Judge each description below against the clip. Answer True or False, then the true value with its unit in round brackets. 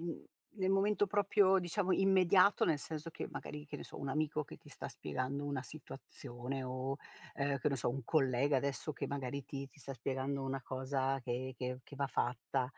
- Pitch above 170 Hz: False (140 Hz)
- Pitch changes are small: False (3.1 semitones)